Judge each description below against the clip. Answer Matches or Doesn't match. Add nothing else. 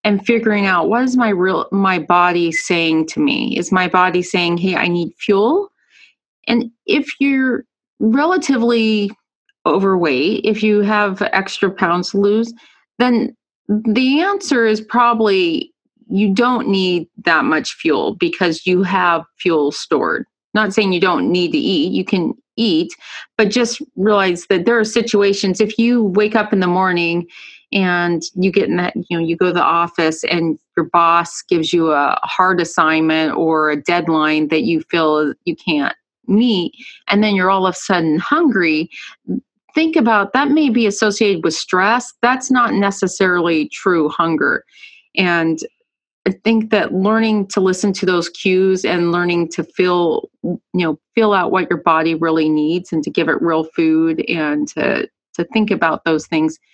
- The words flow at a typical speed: Matches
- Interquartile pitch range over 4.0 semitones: Matches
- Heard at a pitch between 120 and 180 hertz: Doesn't match